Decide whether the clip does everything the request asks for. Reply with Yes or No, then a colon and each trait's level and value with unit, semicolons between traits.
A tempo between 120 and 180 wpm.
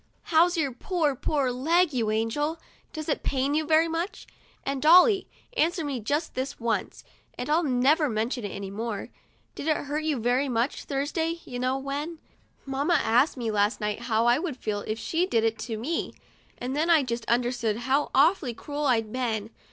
No: average, 190 wpm